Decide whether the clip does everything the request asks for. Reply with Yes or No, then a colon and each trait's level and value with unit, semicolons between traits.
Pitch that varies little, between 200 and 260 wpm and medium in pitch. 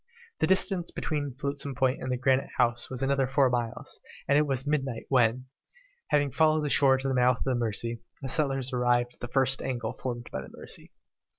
No: narrow, 2.3 semitones; fast, 205 wpm; low, 130 Hz